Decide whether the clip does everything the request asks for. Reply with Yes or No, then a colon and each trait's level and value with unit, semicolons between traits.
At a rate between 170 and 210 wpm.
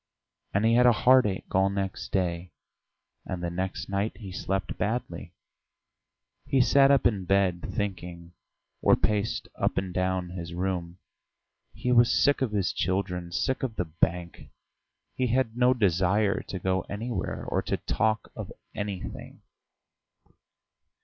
No: average, 145 wpm